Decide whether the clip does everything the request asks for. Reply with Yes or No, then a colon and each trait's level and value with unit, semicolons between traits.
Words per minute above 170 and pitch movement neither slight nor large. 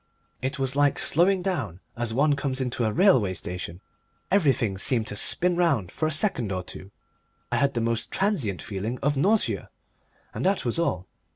No: average, 180 wpm; wide, 7.4 semitones